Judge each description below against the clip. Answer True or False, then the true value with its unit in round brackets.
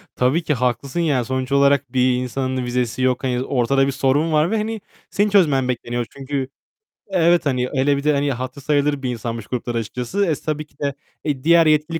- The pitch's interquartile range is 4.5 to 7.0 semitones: False (3.2 semitones)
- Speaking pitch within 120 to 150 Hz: True (135 Hz)